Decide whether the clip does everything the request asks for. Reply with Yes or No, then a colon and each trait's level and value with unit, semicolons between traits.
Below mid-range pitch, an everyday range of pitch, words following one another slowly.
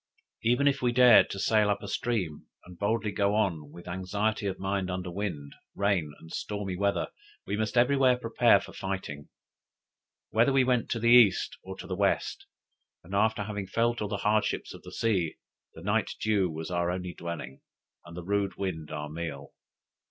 No: low, 100 Hz; average, 3.8 semitones; average, 185 wpm